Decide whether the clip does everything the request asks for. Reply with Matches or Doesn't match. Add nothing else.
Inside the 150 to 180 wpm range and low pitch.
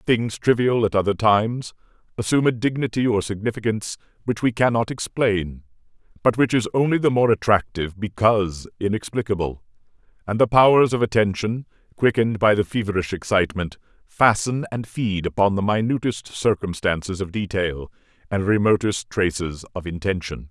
Doesn't match